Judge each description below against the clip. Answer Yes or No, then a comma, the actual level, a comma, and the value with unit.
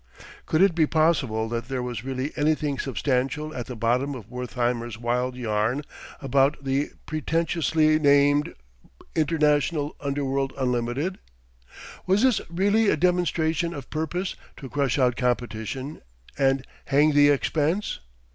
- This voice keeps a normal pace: No, slow, 130 wpm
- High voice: No, medium, 140 Hz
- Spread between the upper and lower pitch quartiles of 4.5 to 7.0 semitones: No, average, 3.8 semitones